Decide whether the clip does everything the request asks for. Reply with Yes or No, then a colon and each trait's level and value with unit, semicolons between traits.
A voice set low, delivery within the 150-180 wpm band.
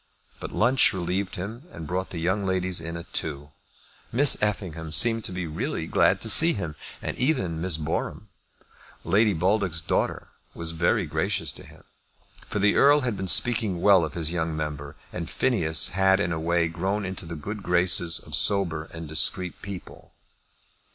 Yes: very low, 90 Hz; average, 175 wpm